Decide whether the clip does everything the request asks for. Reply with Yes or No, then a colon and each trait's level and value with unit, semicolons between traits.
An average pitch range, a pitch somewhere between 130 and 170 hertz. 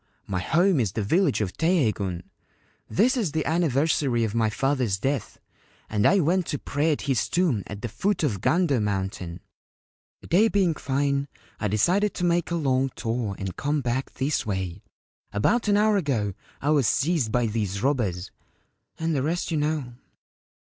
No: wide, 7.5 semitones; medium, 140 Hz